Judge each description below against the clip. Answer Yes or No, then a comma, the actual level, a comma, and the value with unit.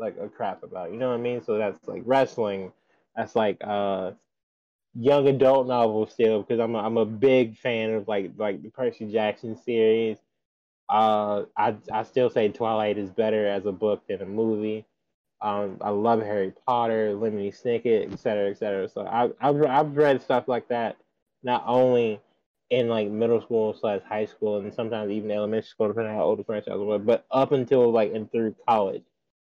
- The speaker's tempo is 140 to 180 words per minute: No, average, 195 wpm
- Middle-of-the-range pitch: No, low, 110 Hz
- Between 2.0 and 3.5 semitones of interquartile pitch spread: Yes, narrow, 2.4 semitones